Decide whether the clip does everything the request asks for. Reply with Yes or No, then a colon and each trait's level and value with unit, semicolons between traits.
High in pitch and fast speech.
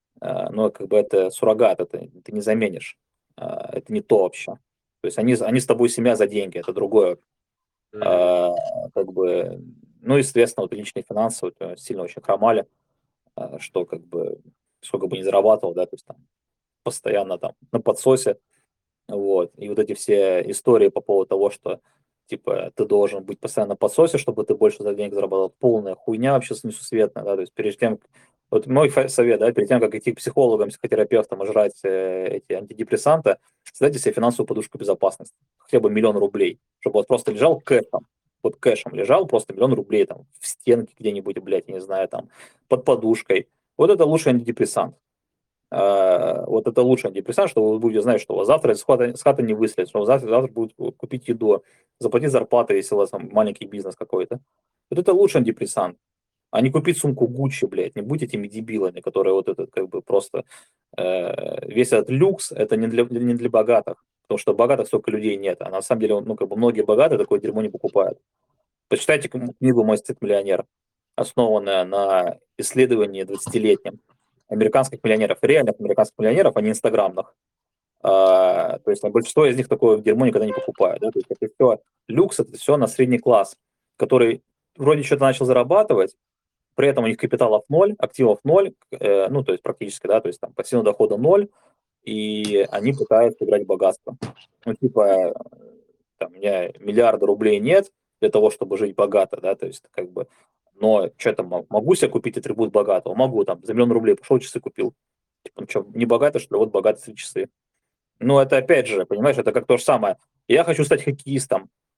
Yes: very high, 335 Hz; fast, 185 wpm